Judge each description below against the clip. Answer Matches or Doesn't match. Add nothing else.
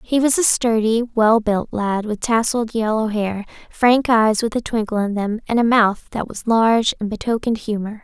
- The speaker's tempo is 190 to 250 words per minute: Matches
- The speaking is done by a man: Doesn't match